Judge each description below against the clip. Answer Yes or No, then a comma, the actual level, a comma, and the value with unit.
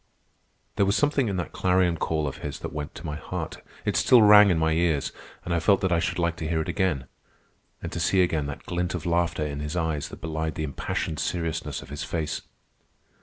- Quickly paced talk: Yes, fast, 220 wpm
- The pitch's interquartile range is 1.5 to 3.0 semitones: Yes, average, 2.7 semitones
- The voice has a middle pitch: No, very low, 80 Hz